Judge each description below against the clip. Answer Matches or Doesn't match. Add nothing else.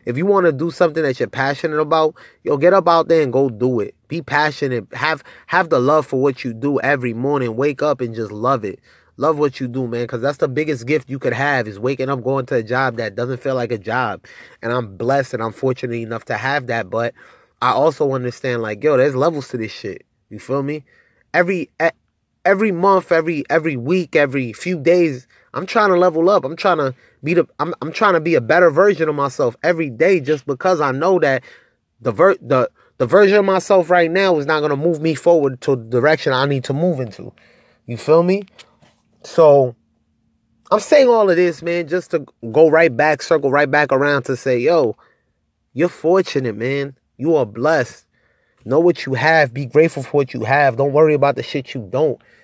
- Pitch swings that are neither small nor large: Matches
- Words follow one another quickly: Matches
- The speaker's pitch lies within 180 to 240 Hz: Doesn't match